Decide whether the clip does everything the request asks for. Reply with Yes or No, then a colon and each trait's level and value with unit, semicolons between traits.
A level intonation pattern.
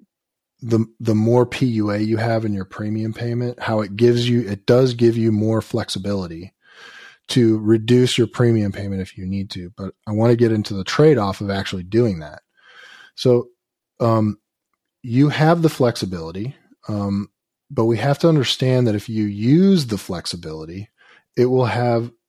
No: average, 3.2 semitones